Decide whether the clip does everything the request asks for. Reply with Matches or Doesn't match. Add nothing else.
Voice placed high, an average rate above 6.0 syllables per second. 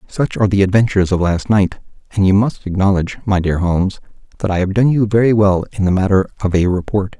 Doesn't match